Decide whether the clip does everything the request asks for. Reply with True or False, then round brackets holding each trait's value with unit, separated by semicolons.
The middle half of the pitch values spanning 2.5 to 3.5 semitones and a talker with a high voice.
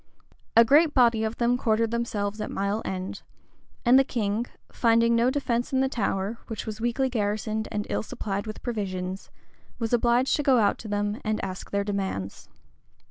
True (2.8 semitones; 220 Hz)